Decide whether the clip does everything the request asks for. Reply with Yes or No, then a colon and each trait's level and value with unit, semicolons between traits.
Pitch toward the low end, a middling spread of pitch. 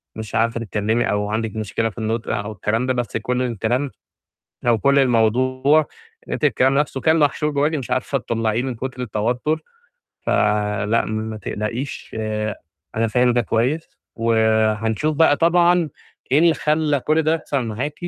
Yes: low, 120 Hz; average, 4.4 semitones